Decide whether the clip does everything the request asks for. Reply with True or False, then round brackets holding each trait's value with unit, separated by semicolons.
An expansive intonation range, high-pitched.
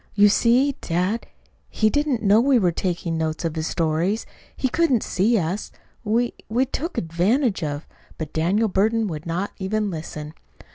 True (5.8 semitones; 200 Hz)